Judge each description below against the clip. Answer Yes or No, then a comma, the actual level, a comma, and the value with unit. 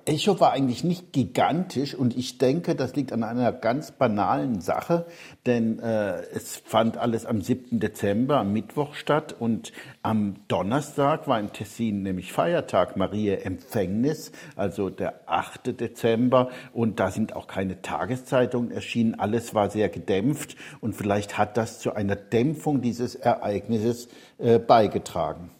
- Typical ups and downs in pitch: Yes, average, 3.6 semitones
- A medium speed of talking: Yes, average, 145 wpm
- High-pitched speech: No, low, 120 Hz